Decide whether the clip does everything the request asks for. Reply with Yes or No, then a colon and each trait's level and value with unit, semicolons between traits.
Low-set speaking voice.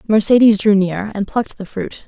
No: high, 205 Hz